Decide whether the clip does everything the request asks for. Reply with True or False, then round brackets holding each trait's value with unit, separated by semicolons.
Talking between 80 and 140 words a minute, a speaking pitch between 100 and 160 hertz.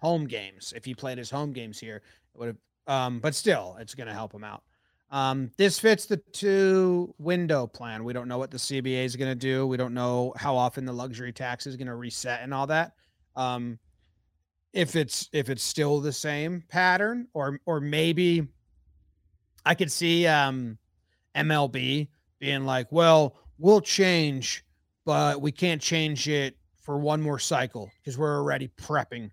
False (180 wpm; 135 Hz)